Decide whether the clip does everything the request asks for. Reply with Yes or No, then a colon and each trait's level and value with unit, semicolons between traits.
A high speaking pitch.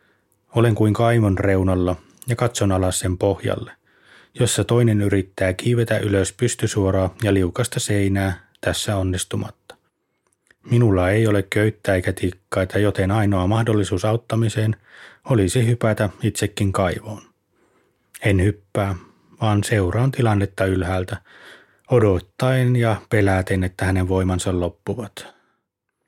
No: low, 100 Hz